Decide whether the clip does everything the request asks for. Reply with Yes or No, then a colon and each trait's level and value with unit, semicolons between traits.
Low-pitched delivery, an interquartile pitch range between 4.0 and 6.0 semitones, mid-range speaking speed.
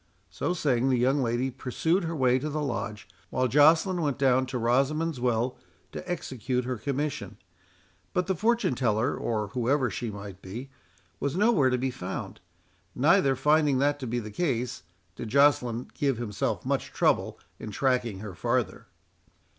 No: low, 130 Hz; average, 3.5 semitones; average, 160 wpm